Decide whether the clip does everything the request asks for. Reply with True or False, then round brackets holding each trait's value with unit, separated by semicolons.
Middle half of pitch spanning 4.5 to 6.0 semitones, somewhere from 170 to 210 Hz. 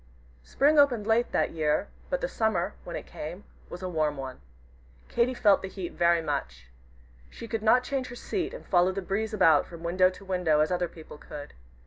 True (5.5 semitones; 185 Hz)